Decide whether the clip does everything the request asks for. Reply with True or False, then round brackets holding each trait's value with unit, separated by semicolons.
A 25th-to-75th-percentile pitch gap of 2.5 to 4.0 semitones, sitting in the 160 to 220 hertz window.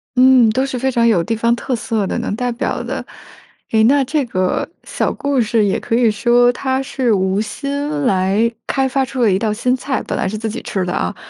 False (3.6 semitones; 235 Hz)